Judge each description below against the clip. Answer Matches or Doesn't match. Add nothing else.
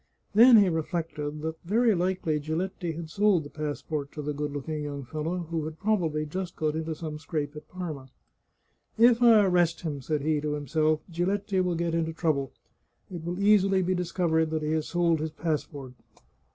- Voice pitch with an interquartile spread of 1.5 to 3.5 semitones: Matches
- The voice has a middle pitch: Matches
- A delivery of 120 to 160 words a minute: Doesn't match